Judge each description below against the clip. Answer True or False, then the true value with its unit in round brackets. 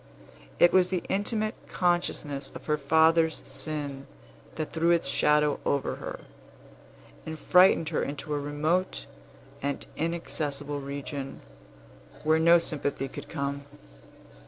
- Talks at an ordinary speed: False (120 wpm)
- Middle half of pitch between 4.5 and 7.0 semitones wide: False (2.9 semitones)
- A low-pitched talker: False (150 Hz)